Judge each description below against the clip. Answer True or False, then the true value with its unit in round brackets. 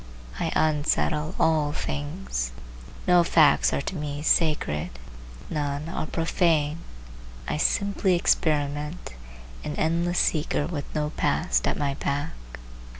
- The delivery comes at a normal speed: False (115 wpm)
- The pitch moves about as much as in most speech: False (2.3 semitones)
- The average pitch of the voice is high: False (150 Hz)